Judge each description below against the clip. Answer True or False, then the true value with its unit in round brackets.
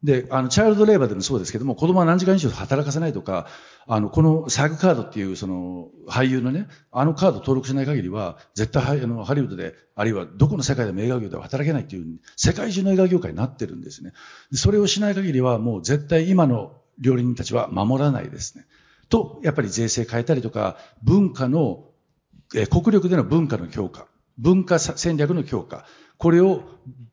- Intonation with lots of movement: True (6.0 semitones)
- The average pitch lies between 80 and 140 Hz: True (135 Hz)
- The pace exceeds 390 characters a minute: True (410 characters per minute)